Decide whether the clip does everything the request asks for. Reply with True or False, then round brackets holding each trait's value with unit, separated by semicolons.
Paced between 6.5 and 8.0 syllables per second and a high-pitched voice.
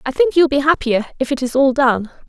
False (5.9 syllables/s; 270 Hz)